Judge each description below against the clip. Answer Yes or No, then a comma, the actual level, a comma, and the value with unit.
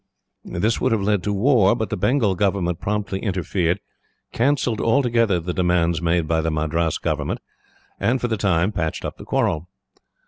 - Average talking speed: Yes, average, 170 wpm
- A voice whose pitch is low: Yes, very low, 95 Hz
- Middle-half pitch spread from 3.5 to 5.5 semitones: Yes, average, 4.7 semitones